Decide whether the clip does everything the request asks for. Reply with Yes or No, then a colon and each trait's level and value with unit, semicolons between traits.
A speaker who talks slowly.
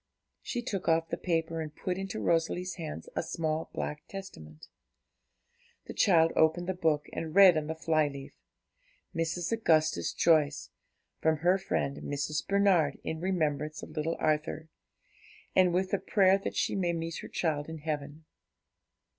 No: average, 155 wpm